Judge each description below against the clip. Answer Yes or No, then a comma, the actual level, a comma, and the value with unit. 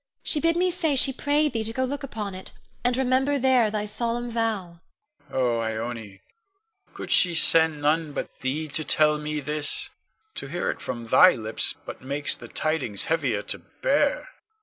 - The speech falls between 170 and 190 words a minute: Yes, average, 180 wpm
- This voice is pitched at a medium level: Yes, medium, 175 Hz